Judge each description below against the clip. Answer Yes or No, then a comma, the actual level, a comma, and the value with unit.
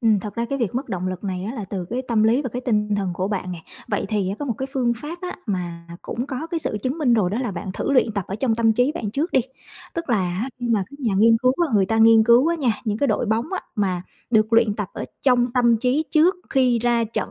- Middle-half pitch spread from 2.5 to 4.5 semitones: Yes, average, 3.9 semitones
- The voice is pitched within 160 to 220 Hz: No, high, 230 Hz